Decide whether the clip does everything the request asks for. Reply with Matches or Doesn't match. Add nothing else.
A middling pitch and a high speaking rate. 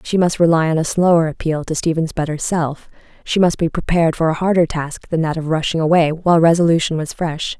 Matches